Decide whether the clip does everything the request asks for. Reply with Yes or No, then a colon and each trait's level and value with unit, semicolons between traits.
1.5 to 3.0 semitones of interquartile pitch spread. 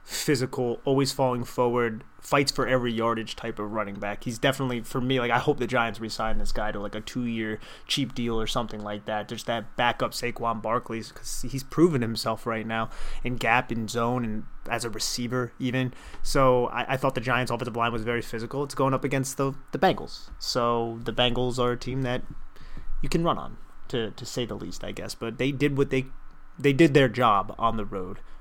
Yes: average, 2.7 semitones